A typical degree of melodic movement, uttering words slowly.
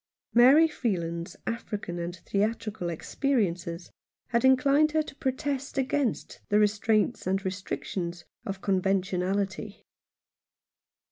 No: wide, 5.8 semitones; slow, 105 wpm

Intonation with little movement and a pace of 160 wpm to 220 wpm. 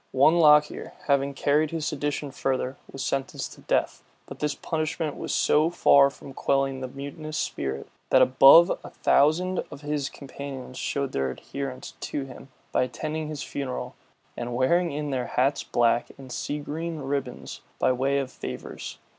Yes: narrow, 2.3 semitones; average, 165 wpm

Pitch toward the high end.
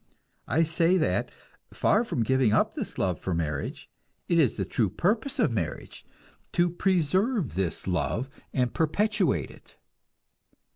No: medium, 145 Hz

